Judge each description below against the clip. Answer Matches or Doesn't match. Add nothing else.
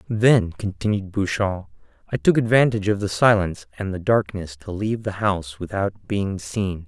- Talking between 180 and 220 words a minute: Doesn't match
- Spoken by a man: Matches